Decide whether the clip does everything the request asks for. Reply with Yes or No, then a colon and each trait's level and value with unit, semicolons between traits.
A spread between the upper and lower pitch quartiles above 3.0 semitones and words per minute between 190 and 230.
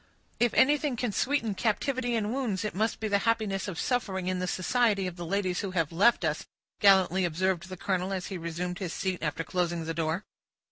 Yes: average, 3.8 semitones; fast, 205 wpm